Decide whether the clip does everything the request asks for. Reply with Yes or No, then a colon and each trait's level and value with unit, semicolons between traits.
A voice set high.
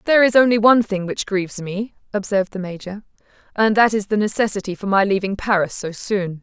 Yes: high, 205 Hz